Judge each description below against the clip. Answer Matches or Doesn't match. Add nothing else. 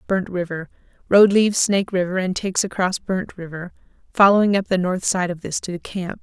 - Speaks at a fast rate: Doesn't match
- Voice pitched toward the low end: Doesn't match